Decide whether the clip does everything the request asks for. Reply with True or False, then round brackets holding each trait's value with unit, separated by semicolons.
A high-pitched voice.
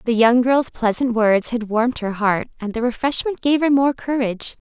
True (240 Hz)